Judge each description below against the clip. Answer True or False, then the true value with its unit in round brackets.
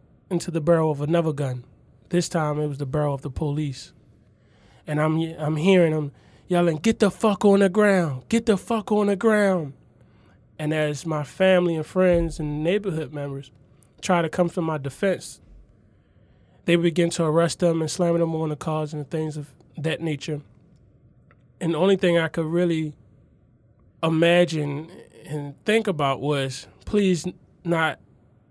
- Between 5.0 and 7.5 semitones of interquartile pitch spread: False (4.0 semitones)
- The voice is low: False (155 Hz)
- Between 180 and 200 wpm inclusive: False (165 wpm)